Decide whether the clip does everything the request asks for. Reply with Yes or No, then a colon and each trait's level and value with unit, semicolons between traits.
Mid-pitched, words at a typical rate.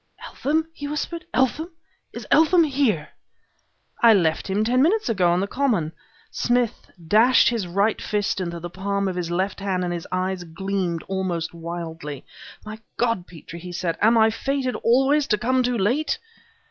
No: high, 200 Hz; average, 170 wpm